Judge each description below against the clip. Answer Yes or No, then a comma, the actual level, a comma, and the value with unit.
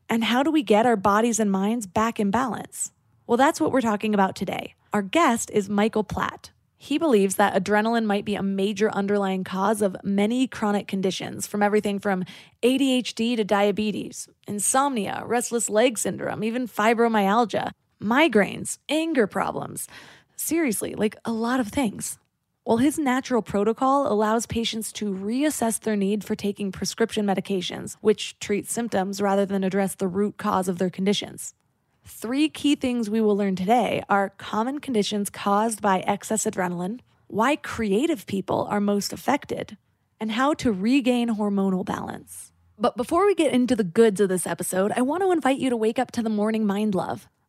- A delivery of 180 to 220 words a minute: No, average, 170 wpm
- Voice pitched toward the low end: No, high, 215 Hz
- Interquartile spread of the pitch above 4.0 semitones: No, average, 3.1 semitones